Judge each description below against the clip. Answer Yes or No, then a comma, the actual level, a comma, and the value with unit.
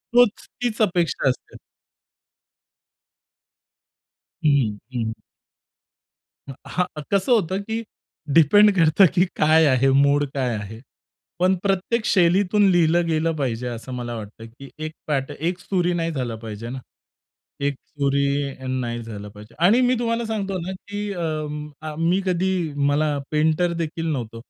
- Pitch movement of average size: No, wide, 6.1 semitones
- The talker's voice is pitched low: No, medium, 155 Hz